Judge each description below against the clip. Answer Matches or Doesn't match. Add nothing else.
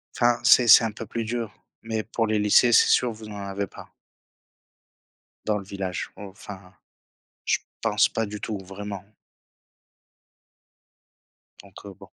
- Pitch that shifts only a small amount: Matches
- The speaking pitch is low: Matches